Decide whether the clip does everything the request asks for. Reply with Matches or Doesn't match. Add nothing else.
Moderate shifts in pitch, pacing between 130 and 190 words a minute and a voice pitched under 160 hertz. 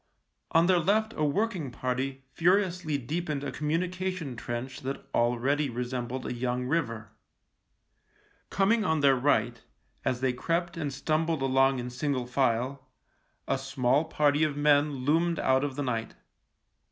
Matches